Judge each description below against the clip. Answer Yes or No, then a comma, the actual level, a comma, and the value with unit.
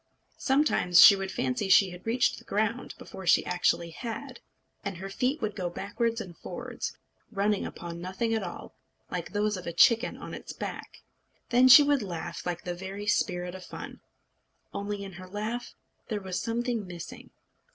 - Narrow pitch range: No, average, 4.1 semitones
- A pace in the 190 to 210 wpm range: No, average, 175 wpm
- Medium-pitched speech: No, high, 200 Hz